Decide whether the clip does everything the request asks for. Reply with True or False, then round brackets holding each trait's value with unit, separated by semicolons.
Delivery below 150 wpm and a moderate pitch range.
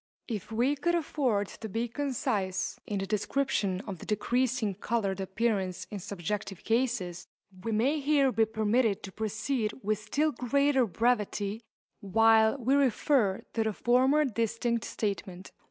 True (140 wpm; 3.9 semitones)